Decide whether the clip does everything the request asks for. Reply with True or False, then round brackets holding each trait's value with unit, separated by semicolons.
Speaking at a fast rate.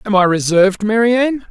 False (160 wpm)